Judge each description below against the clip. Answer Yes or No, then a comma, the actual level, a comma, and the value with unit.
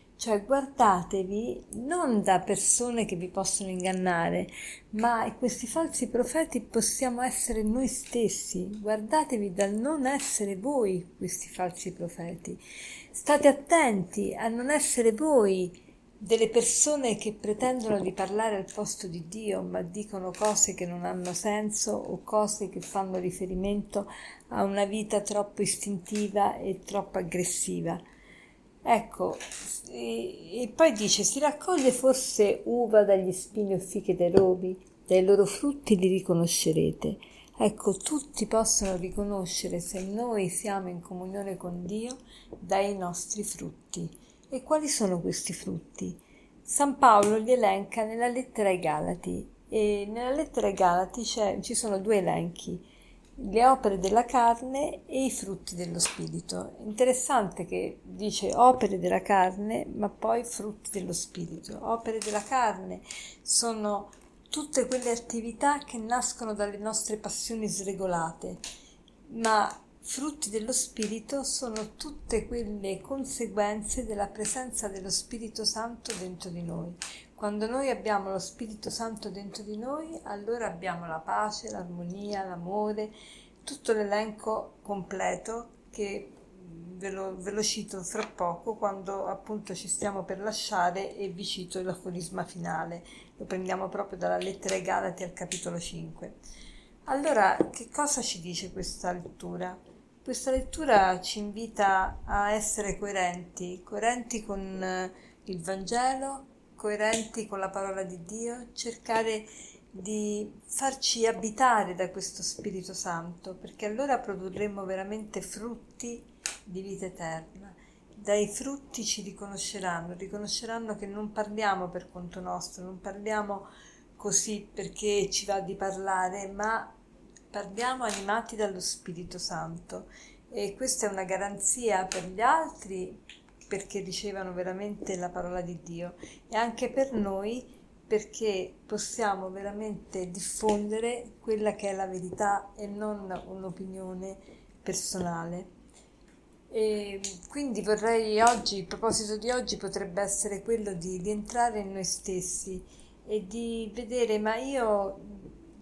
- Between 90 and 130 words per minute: Yes, average, 125 wpm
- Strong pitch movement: No, average, 3.3 semitones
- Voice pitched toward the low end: No, high, 205 Hz